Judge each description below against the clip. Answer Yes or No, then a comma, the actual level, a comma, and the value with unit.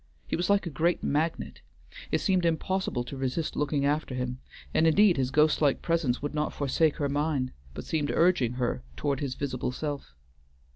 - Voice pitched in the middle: Yes, medium, 145 Hz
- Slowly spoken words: No, average, 185 wpm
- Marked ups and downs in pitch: No, average, 3.6 semitones